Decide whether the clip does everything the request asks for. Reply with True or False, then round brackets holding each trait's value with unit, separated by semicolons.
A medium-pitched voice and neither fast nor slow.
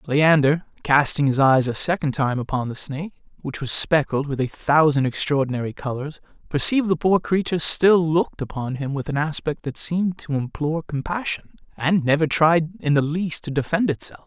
True (150 Hz; 180 wpm)